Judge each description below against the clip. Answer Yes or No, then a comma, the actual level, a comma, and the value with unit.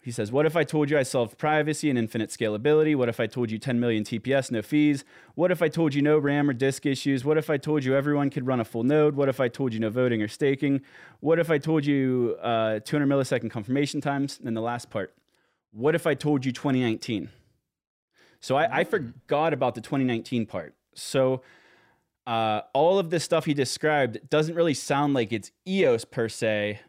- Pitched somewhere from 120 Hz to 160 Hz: Yes, low, 135 Hz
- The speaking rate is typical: No, fast, 220 wpm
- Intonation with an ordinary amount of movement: Yes, average, 4.3 semitones